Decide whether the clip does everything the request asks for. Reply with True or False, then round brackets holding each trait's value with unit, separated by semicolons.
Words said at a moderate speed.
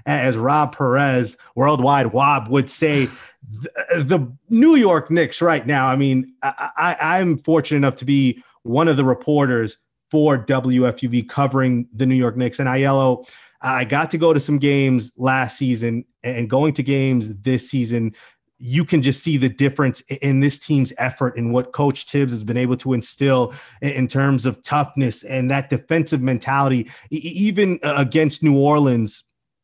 True (170 wpm)